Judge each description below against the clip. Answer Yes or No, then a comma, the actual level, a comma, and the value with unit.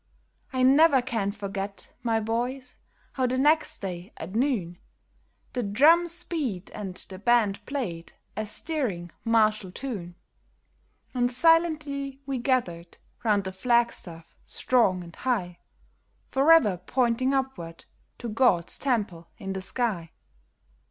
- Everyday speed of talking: No, slow, 125 wpm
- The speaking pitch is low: No, high, 230 Hz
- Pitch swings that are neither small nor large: No, wide, 5.8 semitones